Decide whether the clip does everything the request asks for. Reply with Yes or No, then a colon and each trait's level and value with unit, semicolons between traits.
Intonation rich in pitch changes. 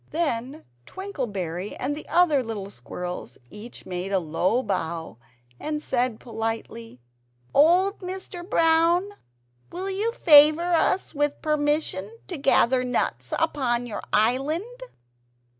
Yes: wide, 7.7 semitones